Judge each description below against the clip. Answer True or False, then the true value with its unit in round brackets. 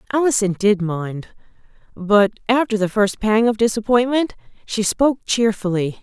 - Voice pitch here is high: True (215 Hz)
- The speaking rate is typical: False (130 wpm)